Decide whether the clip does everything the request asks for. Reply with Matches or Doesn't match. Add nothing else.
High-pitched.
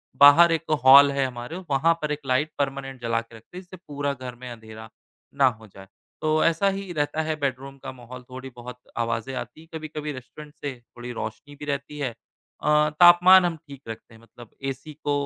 Doesn't match